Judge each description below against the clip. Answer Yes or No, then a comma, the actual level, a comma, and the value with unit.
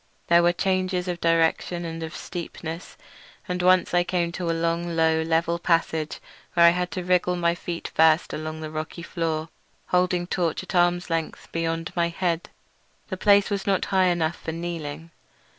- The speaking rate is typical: Yes, average, 175 wpm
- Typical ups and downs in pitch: No, narrow, 1.5 semitones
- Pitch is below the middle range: No, medium, 170 Hz